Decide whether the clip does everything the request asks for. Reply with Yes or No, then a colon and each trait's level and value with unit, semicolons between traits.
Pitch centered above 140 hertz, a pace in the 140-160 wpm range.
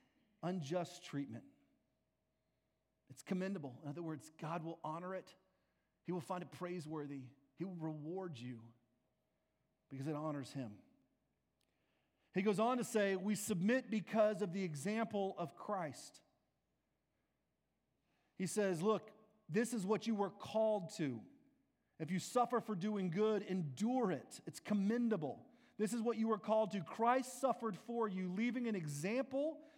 Yes: high, 190 Hz; average, 145 wpm